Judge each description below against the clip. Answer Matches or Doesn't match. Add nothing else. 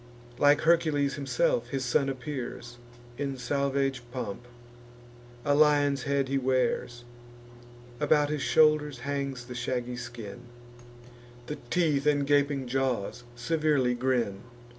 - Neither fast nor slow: Doesn't match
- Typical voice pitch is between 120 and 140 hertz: Matches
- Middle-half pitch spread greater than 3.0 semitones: Doesn't match